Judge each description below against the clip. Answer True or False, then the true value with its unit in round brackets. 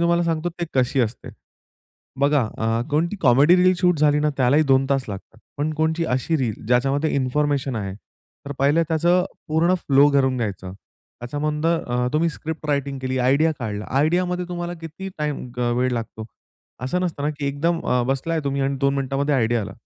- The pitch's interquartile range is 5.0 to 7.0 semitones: False (4.0 semitones)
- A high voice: False (140 Hz)